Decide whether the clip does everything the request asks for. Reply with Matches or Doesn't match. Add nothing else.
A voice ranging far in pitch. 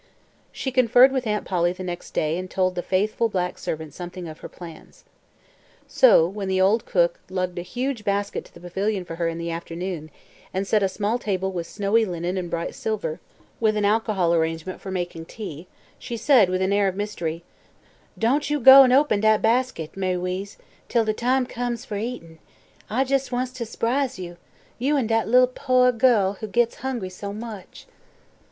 Doesn't match